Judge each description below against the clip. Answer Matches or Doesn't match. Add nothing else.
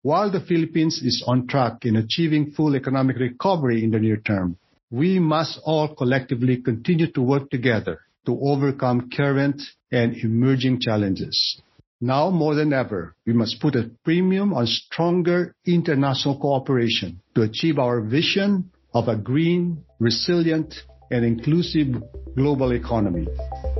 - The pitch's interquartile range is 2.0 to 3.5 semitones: Doesn't match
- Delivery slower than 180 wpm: Matches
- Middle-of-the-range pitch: Doesn't match